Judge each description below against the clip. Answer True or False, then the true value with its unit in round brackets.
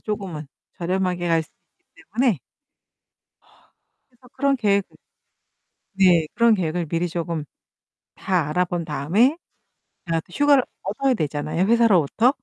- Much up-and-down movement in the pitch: True (5.9 semitones)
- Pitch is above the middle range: False (180 Hz)